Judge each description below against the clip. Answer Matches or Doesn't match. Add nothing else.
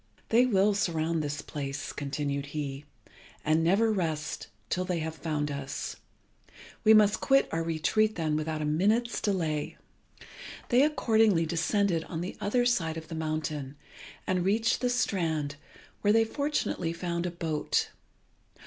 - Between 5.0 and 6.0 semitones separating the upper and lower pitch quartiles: Matches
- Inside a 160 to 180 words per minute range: Doesn't match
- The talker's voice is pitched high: Doesn't match